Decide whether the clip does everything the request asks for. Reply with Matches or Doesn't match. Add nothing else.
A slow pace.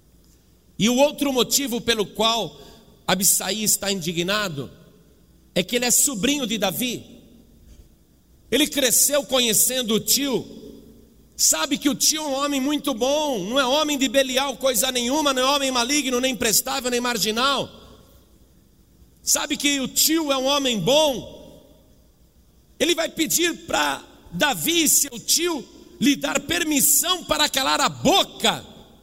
Doesn't match